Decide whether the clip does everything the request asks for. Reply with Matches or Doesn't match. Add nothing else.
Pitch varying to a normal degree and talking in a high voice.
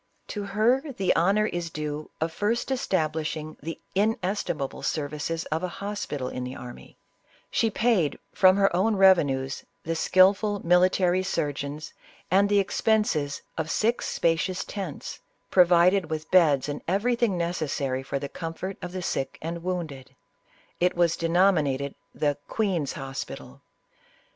Doesn't match